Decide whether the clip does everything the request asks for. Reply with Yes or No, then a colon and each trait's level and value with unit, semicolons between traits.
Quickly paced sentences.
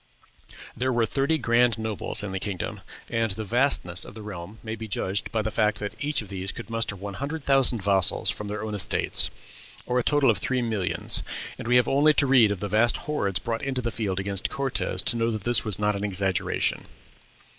Yes: fast, 220 wpm